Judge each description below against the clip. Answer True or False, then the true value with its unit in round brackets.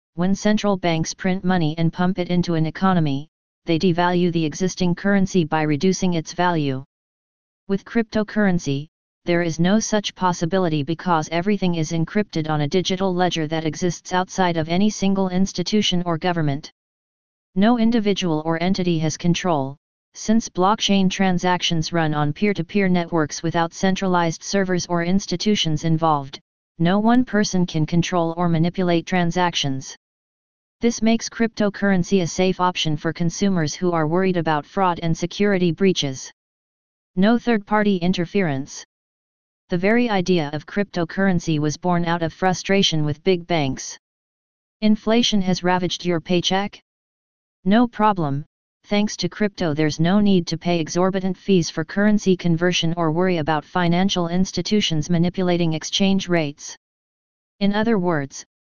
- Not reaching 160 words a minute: True (140 wpm)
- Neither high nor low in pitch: True (180 Hz)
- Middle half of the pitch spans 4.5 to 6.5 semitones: False (2.9 semitones)